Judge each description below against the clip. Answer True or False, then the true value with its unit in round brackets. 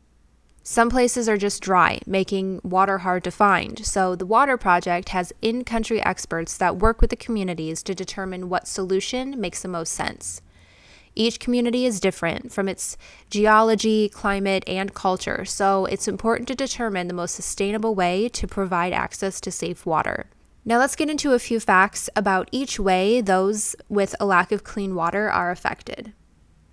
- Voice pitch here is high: True (195 Hz)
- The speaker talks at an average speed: True (170 wpm)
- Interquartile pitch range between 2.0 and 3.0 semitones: False (3.6 semitones)